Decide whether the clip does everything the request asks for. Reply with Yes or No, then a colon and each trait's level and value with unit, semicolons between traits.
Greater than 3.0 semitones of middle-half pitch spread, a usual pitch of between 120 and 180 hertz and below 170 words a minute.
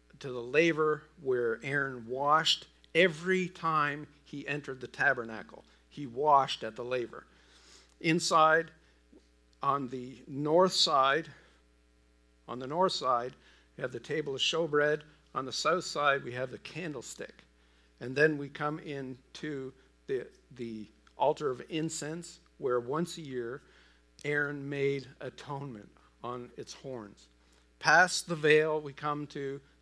Yes: average, 4.7 semitones; medium, 140 Hz; slow, 135 wpm